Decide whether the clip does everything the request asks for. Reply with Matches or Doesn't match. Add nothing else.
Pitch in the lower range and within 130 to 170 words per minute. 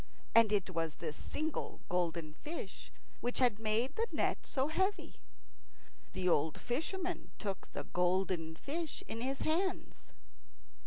Doesn't match